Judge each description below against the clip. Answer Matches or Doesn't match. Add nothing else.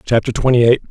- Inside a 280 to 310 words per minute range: Doesn't match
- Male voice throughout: Matches